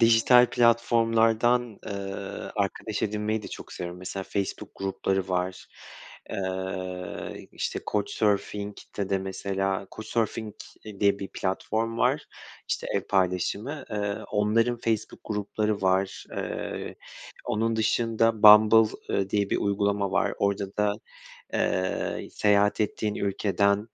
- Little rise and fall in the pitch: Yes, narrow, 2.3 semitones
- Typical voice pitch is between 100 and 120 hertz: Yes, low, 105 Hz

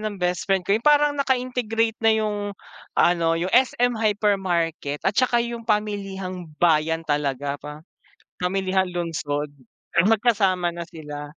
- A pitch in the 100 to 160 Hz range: No, high, 190 Hz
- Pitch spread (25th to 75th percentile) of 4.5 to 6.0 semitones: Yes, average, 5.0 semitones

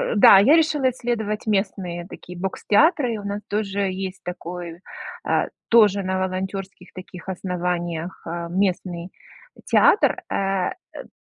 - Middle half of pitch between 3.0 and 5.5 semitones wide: No, narrow, 2.6 semitones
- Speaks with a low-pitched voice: No, high, 190 Hz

